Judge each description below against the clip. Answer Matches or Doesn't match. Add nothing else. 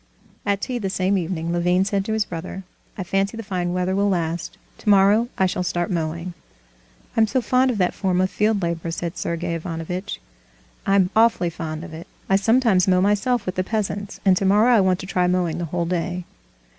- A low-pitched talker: Doesn't match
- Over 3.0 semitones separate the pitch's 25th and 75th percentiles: Doesn't match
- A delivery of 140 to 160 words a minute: Doesn't match